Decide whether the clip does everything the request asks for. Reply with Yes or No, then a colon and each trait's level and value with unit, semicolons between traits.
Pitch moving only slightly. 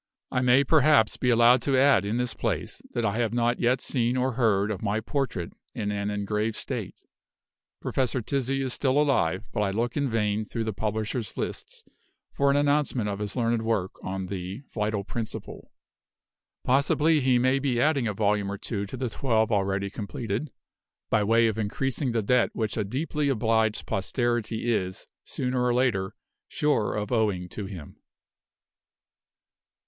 No: average, 3.7 semitones